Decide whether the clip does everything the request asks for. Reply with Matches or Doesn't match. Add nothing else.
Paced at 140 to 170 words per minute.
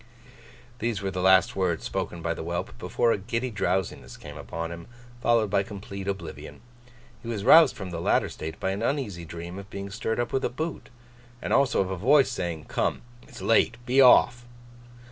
Doesn't match